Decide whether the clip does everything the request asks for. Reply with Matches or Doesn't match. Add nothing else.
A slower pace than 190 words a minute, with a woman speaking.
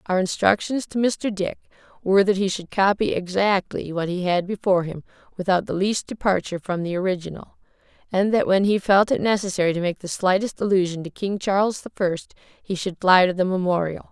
Doesn't match